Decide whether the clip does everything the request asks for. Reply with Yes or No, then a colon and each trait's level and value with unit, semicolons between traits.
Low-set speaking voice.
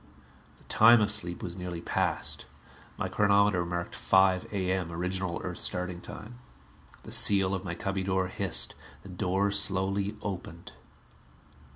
Yes: very low, 95 Hz